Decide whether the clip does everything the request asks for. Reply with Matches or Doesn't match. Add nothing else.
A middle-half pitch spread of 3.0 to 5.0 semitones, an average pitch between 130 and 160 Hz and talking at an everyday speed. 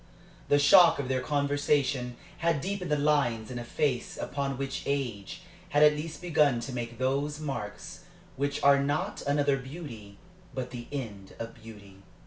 Matches